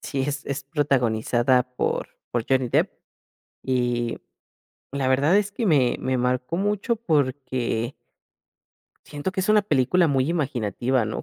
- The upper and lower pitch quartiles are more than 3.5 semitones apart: Yes, average, 4.1 semitones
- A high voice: No, low, 135 Hz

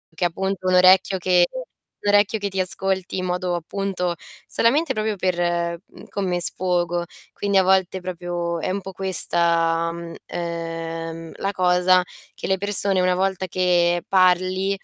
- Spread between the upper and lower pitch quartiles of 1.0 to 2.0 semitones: Yes, narrow, 1.7 semitones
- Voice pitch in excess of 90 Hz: Yes, medium, 185 Hz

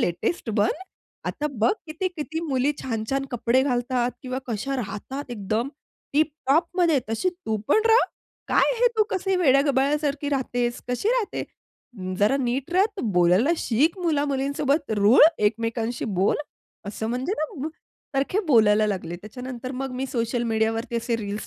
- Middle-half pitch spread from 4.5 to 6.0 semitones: Yes, average, 4.8 semitones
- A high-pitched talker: Yes, very high, 260 Hz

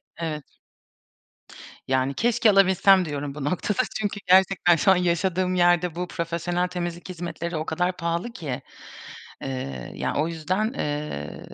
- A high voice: No, medium, 175 Hz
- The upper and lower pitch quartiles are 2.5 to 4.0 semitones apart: Yes, average, 3.2 semitones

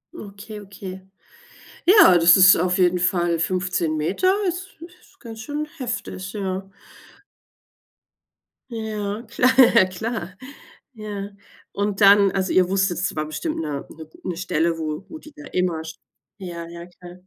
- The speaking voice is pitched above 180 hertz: Yes, high, 190 Hz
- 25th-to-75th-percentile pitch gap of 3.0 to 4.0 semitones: Yes, average, 3.7 semitones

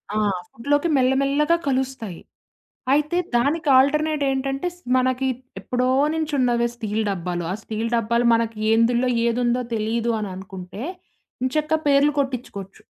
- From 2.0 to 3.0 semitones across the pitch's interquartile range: No, average, 3.7 semitones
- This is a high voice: Yes, very high, 250 Hz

